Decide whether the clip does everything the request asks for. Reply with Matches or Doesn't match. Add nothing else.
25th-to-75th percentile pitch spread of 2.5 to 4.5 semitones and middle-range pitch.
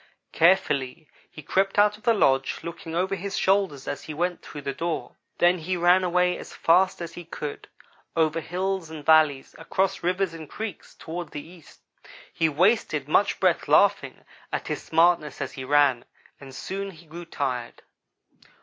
Matches